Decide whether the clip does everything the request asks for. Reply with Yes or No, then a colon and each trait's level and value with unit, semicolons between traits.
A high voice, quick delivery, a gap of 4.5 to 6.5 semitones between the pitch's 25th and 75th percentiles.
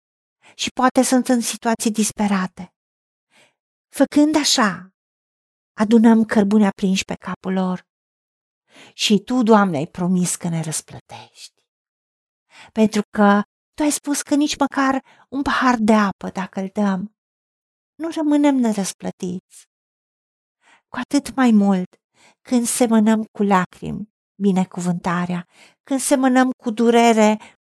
No: high, 220 Hz; slow, 115 wpm; average, 5.0 semitones